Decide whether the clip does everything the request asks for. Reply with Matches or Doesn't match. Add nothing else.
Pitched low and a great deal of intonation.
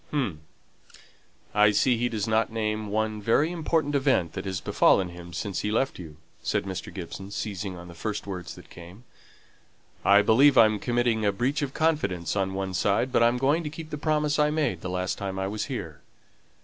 Matches